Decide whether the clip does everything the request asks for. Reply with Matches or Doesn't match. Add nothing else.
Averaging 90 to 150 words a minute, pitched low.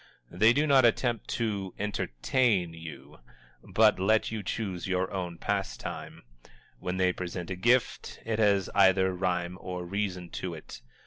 Matches